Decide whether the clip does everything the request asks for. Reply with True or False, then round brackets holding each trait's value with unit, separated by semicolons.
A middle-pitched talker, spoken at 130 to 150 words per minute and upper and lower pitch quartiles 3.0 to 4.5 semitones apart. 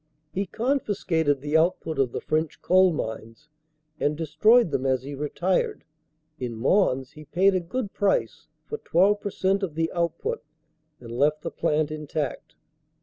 False (160 Hz; 145 wpm; 4.9 semitones)